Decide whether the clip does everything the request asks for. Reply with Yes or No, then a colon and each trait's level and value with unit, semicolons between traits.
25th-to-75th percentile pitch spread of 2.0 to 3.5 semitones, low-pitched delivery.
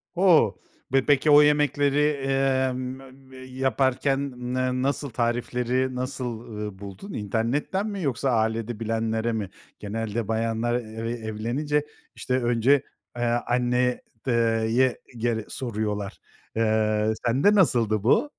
Yes: average, 3.0 semitones; low, 120 Hz